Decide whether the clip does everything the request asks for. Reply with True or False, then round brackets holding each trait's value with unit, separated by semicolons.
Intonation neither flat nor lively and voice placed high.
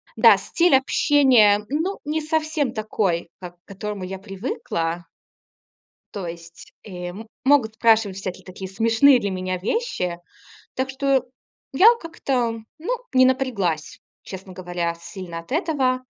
False (6.6 semitones; 215 Hz)